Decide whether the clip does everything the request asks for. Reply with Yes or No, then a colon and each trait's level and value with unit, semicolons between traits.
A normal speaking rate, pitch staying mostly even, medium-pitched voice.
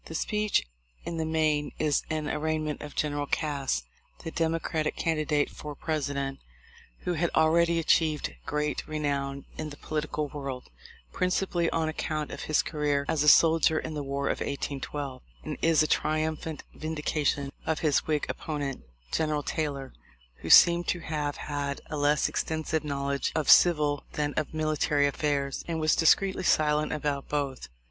Yes: average, 155 wpm; narrow, 1.7 semitones; medium, 150 Hz